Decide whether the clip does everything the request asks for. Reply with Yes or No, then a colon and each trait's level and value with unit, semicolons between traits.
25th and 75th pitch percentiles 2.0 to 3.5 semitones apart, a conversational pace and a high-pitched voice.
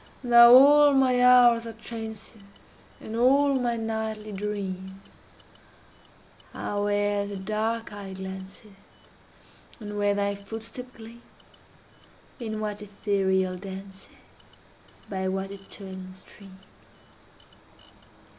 No: average, 2.9 semitones; slow, 100 wpm; high, 210 Hz